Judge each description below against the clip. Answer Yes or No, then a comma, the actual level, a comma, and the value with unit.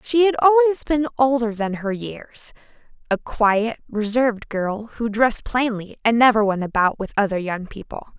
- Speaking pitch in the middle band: No, high, 230 Hz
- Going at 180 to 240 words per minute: No, average, 160 wpm